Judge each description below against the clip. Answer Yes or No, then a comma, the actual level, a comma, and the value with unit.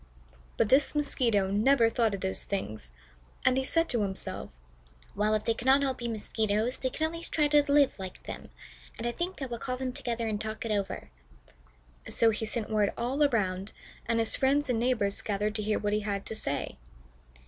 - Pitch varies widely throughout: No, average, 4.1 semitones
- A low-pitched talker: No, high, 230 Hz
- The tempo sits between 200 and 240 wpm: Yes, fast, 205 wpm